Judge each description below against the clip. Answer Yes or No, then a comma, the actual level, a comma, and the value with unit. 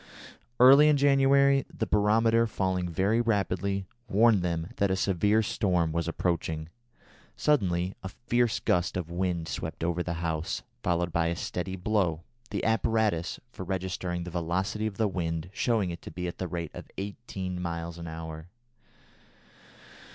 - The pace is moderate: Yes, average, 155 wpm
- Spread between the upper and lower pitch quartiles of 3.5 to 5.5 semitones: Yes, average, 4.0 semitones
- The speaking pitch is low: Yes, very low, 95 Hz